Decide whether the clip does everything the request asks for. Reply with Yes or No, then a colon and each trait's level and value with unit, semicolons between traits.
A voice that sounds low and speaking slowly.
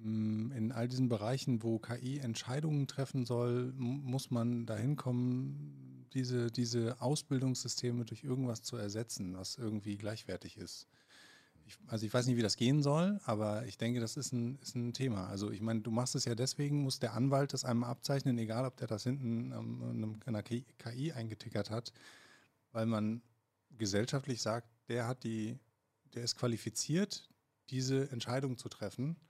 No: low, 120 Hz; average, 165 wpm